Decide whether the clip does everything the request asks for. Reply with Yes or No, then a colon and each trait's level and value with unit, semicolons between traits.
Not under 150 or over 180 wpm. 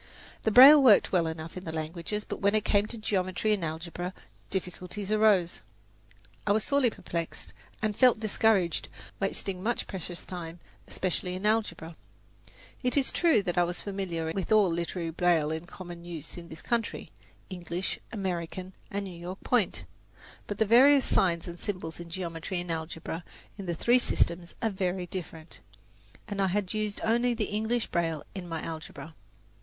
Yes: average, 170 wpm